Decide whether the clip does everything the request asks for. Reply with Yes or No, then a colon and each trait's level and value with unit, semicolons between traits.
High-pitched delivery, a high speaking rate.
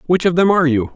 No: medium, 165 Hz; fast, 315 wpm